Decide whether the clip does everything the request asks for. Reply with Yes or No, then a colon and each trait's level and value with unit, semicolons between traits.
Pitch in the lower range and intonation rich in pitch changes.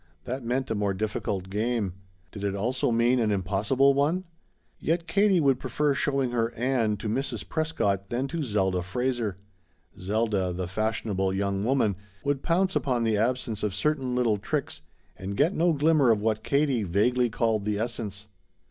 No: low, 115 Hz; average, 4.9 semitones